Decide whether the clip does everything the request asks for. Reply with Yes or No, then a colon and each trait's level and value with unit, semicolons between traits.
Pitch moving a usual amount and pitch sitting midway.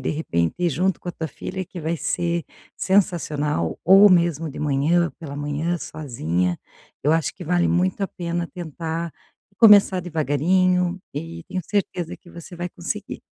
Yes: average, 3.1 semitones; medium, 170 Hz